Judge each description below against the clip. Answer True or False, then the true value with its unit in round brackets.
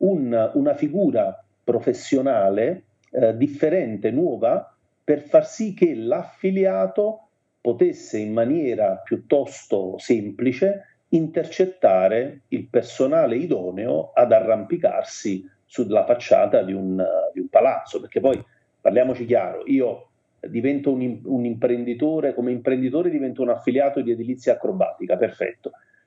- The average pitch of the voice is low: False (150 Hz)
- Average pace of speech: False (110 wpm)